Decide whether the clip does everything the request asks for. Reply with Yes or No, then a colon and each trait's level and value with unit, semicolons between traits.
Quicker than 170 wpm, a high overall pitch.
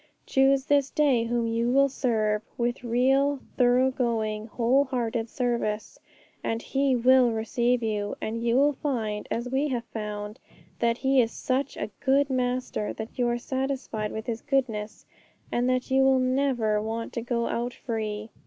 No: average, 165 wpm; high, 240 Hz